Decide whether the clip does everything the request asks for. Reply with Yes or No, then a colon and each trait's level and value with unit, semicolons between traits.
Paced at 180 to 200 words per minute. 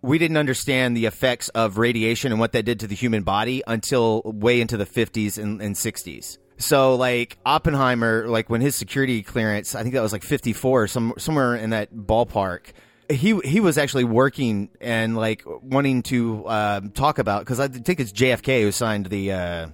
Yes: average, 190 wpm